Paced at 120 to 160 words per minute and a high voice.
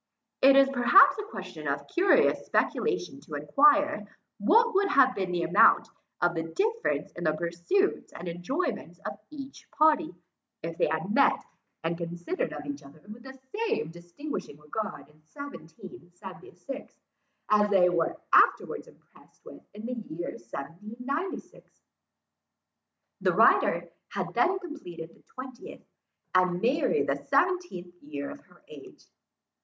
Yes: slow, 135 wpm; high, 215 Hz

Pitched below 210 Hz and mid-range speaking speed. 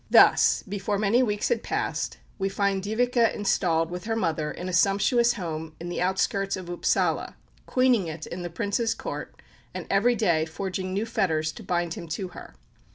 Yes: high, 190 Hz; average, 180 wpm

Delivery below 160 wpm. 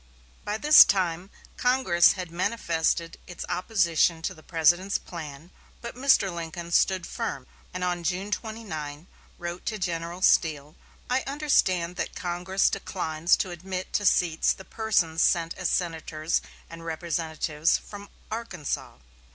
Yes: slow, 135 wpm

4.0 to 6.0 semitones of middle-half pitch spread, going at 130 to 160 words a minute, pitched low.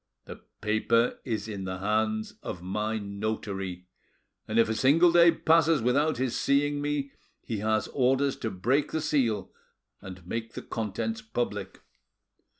Yes: average, 5.1 semitones; average, 150 wpm; low, 115 Hz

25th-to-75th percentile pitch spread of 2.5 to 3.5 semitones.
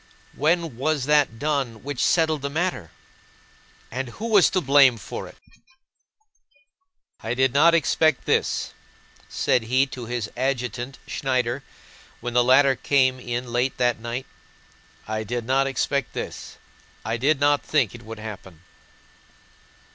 Yes: average, 3.1 semitones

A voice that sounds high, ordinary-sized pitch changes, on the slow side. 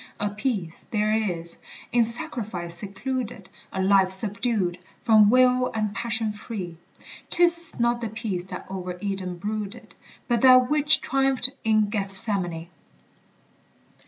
Yes: high, 215 Hz; average, 4.1 semitones; slow, 125 wpm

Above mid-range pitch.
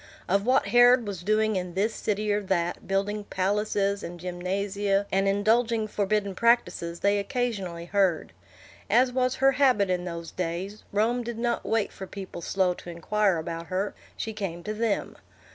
Yes: high, 200 Hz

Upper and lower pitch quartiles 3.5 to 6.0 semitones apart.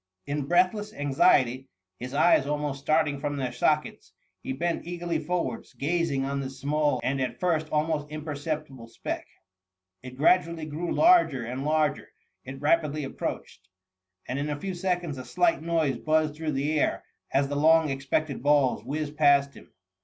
No: average, 2.8 semitones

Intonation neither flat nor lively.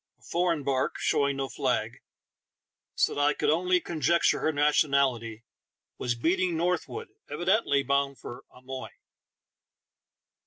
Yes: average, 4.2 semitones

